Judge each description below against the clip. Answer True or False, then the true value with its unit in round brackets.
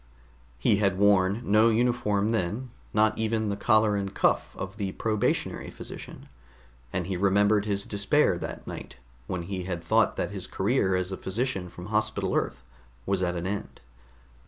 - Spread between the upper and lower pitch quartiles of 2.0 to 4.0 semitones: True (2.4 semitones)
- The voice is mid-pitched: False (100 Hz)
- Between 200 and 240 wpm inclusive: False (165 wpm)